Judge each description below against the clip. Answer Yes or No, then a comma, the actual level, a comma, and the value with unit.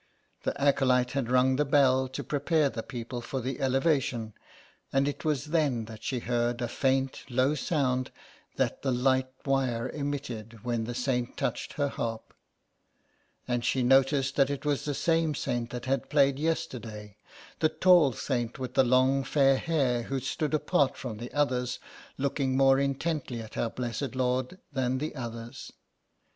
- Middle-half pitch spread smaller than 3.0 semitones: Yes, narrow, 2.5 semitones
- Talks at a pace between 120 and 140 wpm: No, average, 165 wpm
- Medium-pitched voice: No, low, 130 Hz